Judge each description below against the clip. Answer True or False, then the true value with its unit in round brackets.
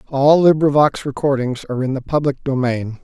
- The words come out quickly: False (160 wpm)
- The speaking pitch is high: False (135 Hz)